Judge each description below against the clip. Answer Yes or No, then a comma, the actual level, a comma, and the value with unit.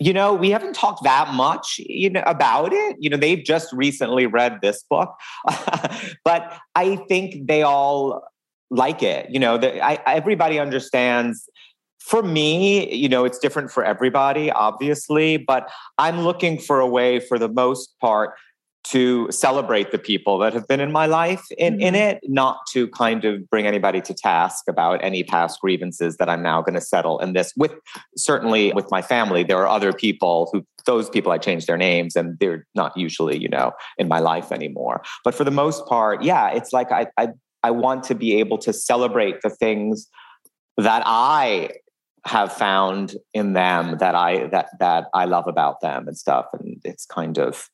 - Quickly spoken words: No, average, 185 wpm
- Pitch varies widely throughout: Yes, wide, 7.5 semitones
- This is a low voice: Yes, low, 130 Hz